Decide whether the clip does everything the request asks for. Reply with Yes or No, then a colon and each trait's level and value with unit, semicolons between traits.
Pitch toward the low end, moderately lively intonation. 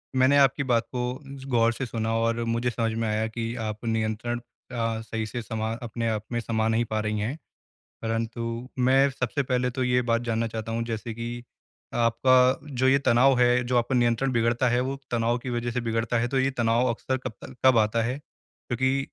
No: low, 120 Hz; narrow, 1.8 semitones